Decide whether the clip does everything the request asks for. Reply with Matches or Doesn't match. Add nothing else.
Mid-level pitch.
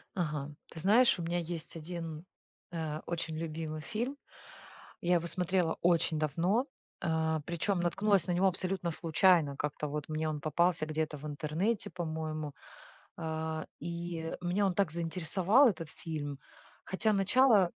Matches